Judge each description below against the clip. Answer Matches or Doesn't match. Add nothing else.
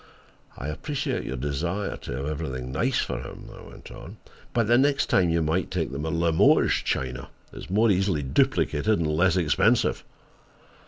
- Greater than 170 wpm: Doesn't match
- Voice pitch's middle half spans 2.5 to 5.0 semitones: Doesn't match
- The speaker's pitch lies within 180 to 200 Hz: Doesn't match